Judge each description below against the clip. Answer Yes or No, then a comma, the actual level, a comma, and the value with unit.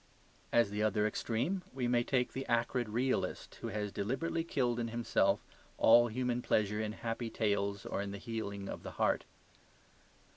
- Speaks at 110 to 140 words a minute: No, average, 170 wpm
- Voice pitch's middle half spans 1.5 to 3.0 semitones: Yes, average, 2.7 semitones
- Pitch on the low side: Yes, low, 115 Hz